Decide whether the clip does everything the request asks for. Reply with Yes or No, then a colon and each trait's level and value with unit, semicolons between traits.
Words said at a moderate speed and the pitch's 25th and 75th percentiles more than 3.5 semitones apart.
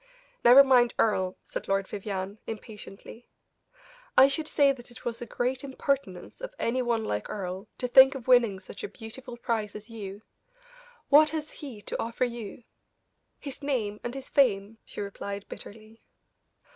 Yes: average, 160 wpm; average, 4.3 semitones